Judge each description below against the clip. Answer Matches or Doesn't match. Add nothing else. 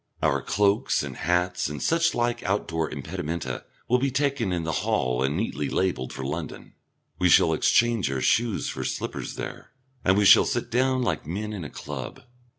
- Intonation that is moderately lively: Doesn't match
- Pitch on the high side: Doesn't match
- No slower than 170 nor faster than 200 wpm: Matches